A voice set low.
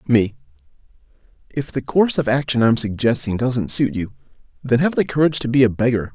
Yes: low, 125 Hz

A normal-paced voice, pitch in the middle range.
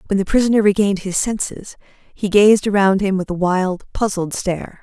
No: average, 185 wpm; high, 195 Hz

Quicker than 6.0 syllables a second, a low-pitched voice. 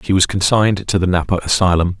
Yes: 6.5 syllables/s; very low, 90 Hz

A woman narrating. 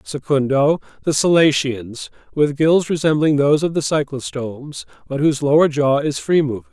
No: male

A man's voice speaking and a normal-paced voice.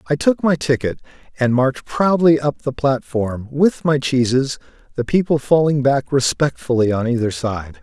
Yes: male; average, 160 wpm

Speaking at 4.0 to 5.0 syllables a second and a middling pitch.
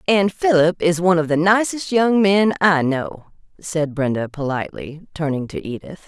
Yes: 4.9 syllables/s; medium, 170 Hz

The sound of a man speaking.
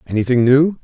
Yes: male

